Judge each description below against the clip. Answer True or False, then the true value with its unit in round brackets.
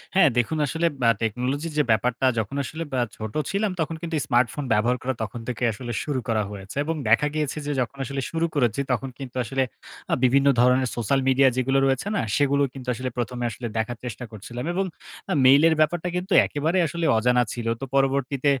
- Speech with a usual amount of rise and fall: True (3.4 semitones)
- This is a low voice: True (130 Hz)